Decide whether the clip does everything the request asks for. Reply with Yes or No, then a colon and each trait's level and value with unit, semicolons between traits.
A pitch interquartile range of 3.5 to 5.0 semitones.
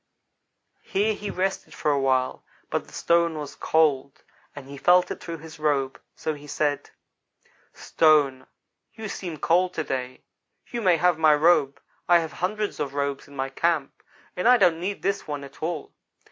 Yes: average, 4.0 semitones